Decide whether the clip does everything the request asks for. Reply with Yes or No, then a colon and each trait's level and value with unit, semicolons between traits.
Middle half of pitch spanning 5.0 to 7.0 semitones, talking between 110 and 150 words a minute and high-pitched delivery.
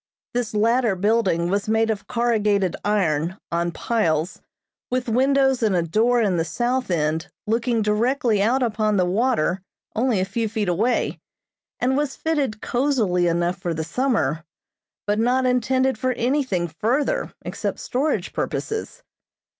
Yes: average, 5.3 semitones; average, 145 wpm; high, 220 Hz